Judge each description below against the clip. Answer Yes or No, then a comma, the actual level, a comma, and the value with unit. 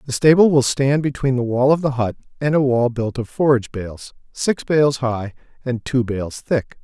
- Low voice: Yes, low, 130 Hz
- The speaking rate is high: Yes, fast, 210 wpm